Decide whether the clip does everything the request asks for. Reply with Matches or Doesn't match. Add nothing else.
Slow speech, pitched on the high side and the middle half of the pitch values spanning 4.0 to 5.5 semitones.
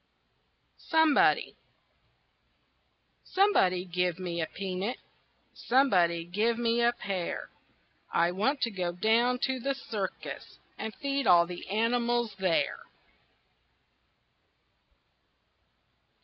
Matches